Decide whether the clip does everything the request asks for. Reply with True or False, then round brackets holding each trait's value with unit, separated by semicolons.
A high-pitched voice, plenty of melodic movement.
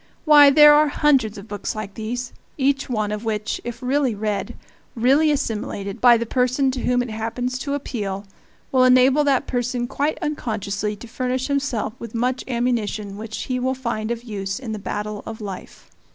False (240 Hz; 3.5 semitones)